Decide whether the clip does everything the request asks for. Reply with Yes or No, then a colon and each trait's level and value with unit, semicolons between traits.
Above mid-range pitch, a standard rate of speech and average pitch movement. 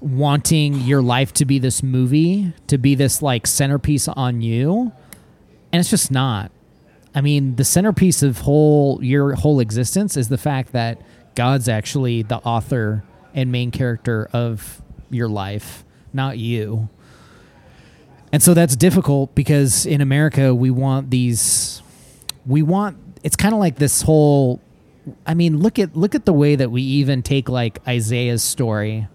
No: low, 135 Hz; average, 155 wpm; average, 3.6 semitones